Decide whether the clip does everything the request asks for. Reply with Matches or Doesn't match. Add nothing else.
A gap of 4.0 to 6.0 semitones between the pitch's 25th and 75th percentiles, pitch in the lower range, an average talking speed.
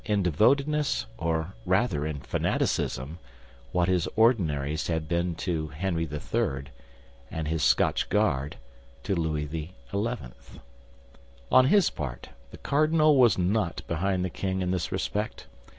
Doesn't match